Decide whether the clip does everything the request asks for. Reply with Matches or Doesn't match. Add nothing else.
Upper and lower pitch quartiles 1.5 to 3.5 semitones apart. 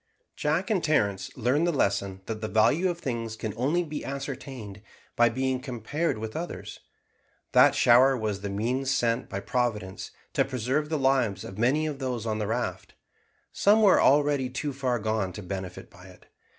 Doesn't match